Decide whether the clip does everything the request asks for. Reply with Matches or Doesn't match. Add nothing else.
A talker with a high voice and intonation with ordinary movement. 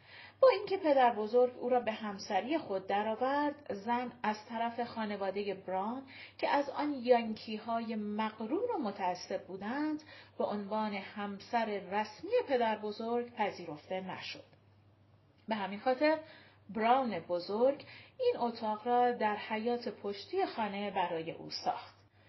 Matches